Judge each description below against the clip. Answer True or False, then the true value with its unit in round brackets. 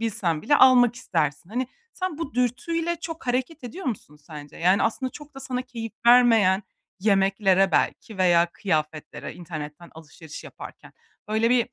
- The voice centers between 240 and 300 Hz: False (220 Hz)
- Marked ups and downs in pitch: True (6.7 semitones)